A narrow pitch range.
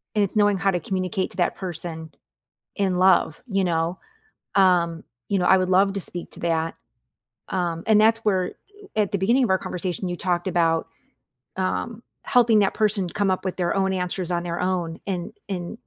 Yes: narrow, 2.2 semitones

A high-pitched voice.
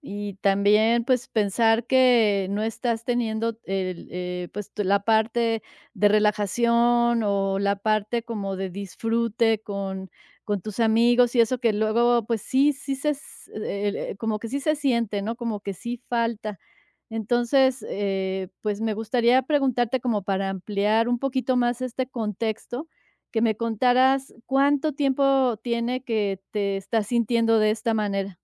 Yes: high, 225 Hz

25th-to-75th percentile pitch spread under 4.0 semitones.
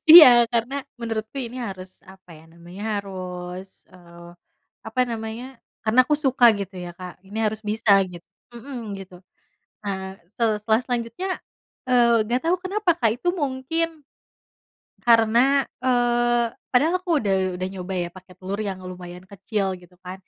No: average, 4.9 semitones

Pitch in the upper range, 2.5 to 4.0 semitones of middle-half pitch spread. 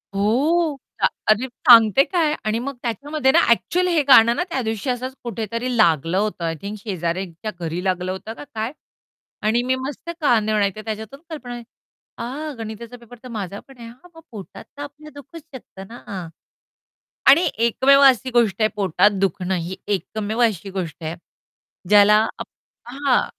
No: high, 230 Hz; average, 4.9 semitones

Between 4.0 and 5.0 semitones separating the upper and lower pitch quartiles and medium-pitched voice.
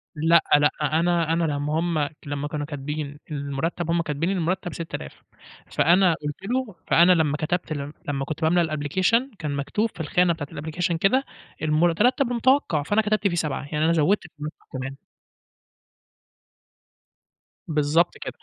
No: average, 3.2 semitones; medium, 160 Hz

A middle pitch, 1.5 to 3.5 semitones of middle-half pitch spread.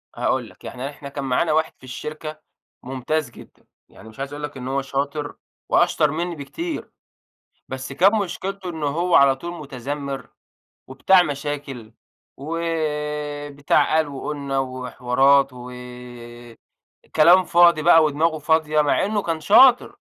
Yes: medium, 150 Hz; average, 3.0 semitones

